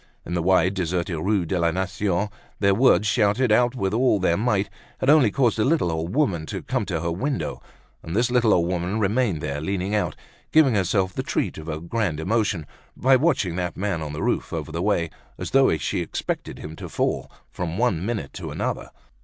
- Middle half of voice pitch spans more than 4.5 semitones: Yes, average, 5.1 semitones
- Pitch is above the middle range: No, very low, 95 Hz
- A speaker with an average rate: No, fast, 210 wpm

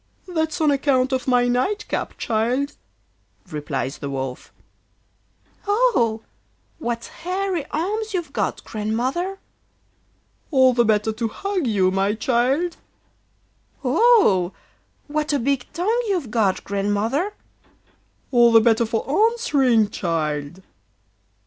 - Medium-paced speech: No, slow, 110 wpm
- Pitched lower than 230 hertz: No, very high, 250 Hz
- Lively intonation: Yes, wide, 7.7 semitones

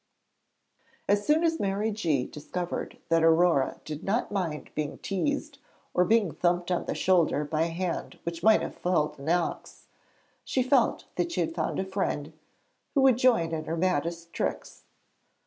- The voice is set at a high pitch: No, medium, 180 Hz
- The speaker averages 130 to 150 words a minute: No, average, 165 wpm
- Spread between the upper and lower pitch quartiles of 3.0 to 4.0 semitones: No, average, 5.0 semitones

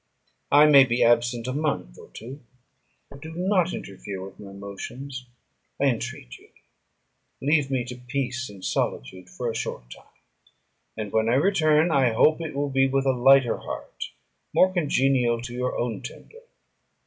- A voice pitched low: Yes, low, 130 Hz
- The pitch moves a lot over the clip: No, average, 3.9 semitones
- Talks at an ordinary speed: Yes, average, 165 wpm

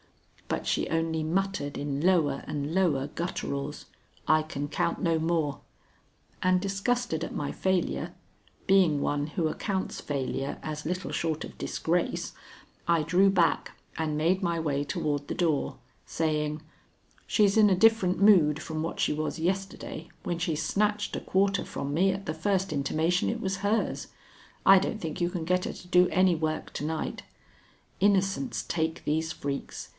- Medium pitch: Yes, medium, 165 Hz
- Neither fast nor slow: Yes, average, 160 wpm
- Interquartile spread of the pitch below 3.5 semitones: No, average, 3.8 semitones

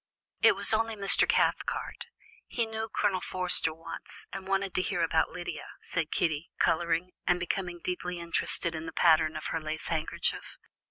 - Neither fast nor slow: Yes, average, 165 wpm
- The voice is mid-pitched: Yes, medium, 175 Hz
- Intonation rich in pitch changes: No, average, 2.8 semitones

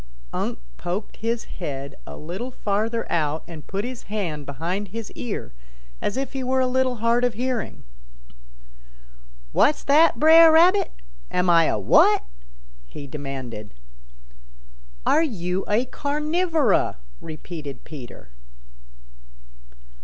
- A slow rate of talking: Yes, slow, 120 wpm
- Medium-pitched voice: No, high, 210 Hz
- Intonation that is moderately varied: No, wide, 8.4 semitones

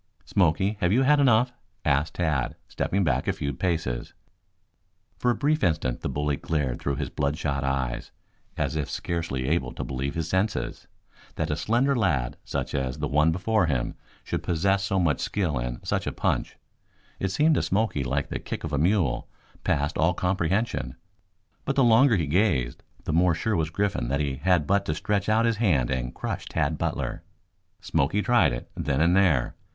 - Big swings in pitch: Yes, wide, 6.3 semitones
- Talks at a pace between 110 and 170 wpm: No, average, 185 wpm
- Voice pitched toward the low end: Yes, very low, 80 Hz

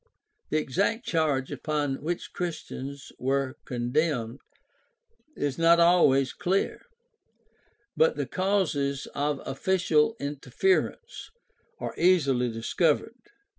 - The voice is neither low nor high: Yes, medium, 150 Hz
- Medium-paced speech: No, slow, 95 wpm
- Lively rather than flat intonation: No, average, 4.6 semitones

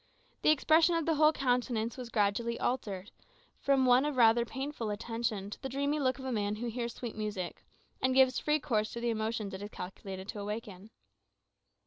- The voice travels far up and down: No, average, 3.9 semitones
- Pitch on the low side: No, high, 235 Hz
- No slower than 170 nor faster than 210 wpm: Yes, average, 190 wpm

